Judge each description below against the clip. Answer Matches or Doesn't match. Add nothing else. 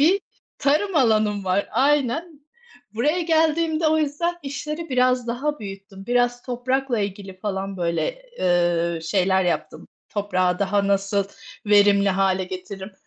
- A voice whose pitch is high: Matches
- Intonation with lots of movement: Matches